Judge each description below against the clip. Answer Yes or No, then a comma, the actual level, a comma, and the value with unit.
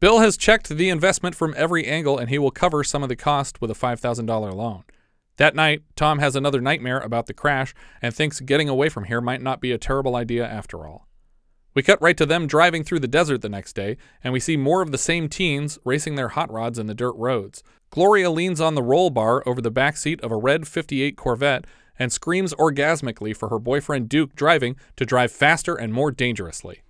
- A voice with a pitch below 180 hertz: Yes, medium, 140 Hz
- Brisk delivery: Yes, fast, 225 wpm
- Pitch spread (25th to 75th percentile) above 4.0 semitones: Yes, average, 4.5 semitones